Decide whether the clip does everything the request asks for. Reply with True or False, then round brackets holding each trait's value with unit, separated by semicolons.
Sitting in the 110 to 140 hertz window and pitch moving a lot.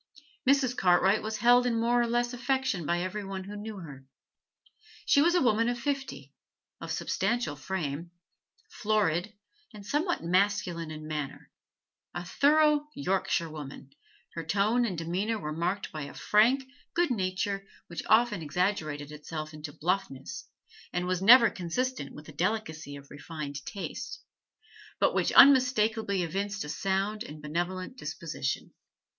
False (195 Hz; 6.6 semitones)